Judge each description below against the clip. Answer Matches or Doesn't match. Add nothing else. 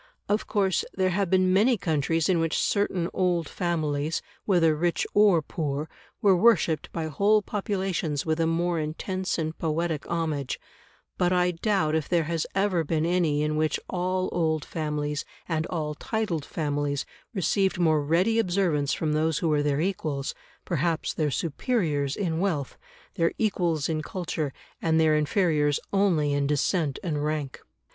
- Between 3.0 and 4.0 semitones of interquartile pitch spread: Matches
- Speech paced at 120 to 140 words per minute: Doesn't match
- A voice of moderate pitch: Matches